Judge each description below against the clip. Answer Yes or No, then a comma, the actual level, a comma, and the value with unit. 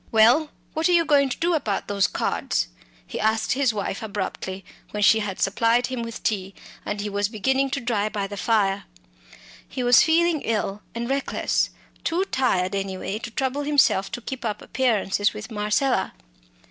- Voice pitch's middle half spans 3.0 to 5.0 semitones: Yes, average, 4.6 semitones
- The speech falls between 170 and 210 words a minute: Yes, average, 175 wpm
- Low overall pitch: No, high, 225 Hz